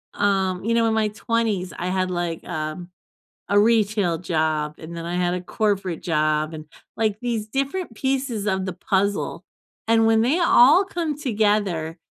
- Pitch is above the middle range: Yes, high, 200 Hz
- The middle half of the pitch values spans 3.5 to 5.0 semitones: Yes, average, 4.7 semitones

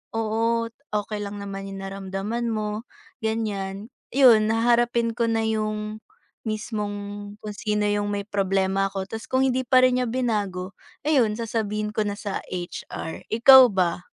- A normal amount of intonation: No, narrow, 2.3 semitones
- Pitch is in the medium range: No, high, 215 Hz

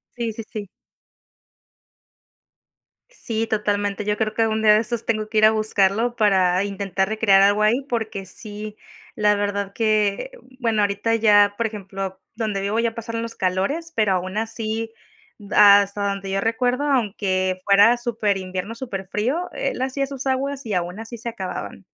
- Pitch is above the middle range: Yes, high, 215 Hz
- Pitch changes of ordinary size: No, narrow, 2.3 semitones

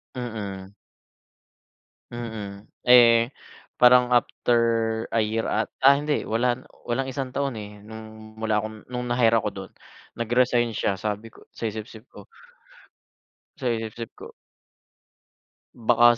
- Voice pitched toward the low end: Yes, low, 115 Hz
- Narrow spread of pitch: Yes, narrow, 2.0 semitones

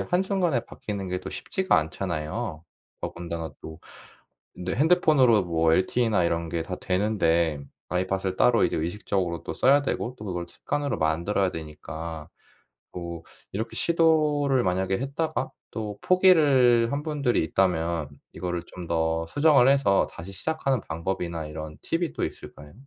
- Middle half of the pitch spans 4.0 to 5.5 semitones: No, wide, 8.3 semitones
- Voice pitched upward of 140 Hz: No, very low, 95 Hz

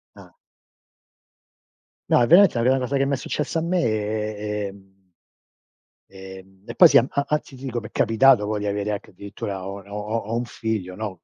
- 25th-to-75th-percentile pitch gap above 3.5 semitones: Yes, average, 4.2 semitones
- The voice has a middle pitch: No, low, 110 Hz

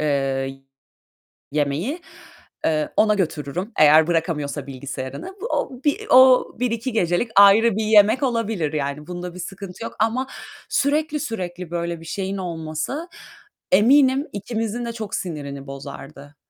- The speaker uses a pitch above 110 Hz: Yes, medium, 185 Hz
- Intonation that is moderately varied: No, wide, 7.2 semitones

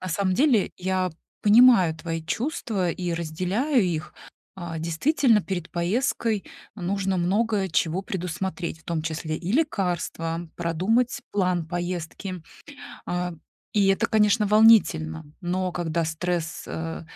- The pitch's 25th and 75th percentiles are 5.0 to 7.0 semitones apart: No, average, 3.6 semitones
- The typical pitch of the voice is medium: Yes, medium, 180 Hz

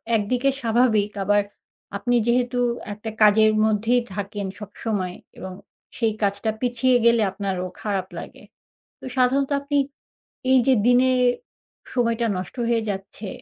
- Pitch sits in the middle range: No, high, 220 Hz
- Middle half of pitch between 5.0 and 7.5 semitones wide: No, average, 3.3 semitones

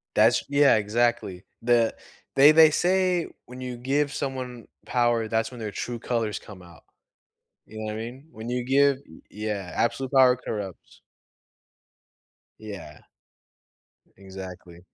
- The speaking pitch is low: Yes, low, 120 Hz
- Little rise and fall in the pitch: No, average, 3.8 semitones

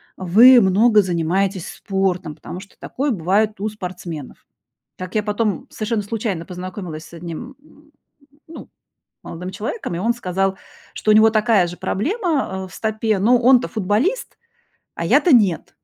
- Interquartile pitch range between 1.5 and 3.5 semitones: No, average, 4.0 semitones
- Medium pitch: No, high, 205 Hz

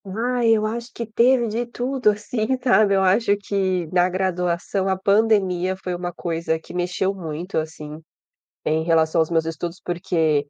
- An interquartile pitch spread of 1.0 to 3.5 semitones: No, average, 3.9 semitones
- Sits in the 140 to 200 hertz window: Yes, medium, 185 Hz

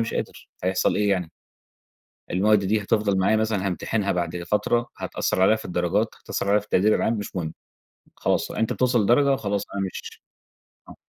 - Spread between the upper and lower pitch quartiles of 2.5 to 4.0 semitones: Yes, average, 2.8 semitones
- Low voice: Yes, low, 100 Hz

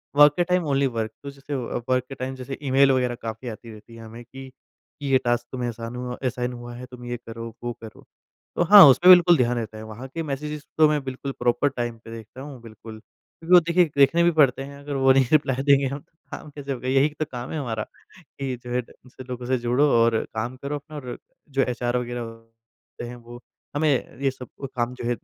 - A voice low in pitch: Yes, low, 130 Hz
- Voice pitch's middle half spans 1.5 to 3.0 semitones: Yes, average, 2.7 semitones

